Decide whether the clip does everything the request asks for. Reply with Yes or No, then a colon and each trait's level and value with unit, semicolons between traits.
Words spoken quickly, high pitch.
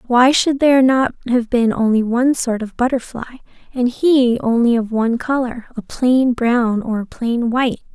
No: average, 180 wpm; high, 240 Hz